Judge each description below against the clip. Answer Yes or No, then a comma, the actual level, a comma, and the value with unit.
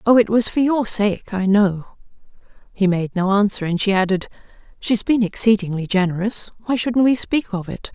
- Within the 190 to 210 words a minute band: No, average, 180 wpm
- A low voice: No, high, 205 Hz